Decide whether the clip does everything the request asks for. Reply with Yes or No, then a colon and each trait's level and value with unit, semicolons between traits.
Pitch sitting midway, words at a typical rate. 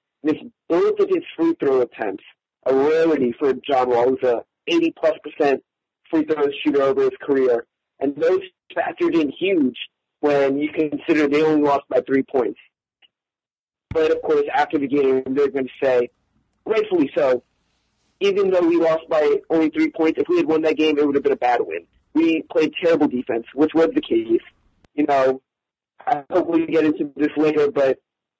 Yes: medium, 160 Hz; average, 185 wpm